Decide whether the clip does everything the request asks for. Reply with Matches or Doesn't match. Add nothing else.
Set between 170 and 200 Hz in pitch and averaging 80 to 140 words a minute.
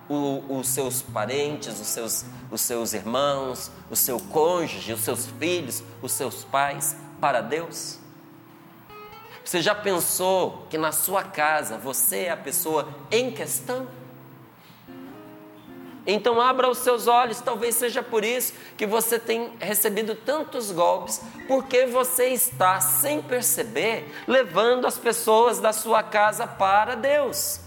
Matches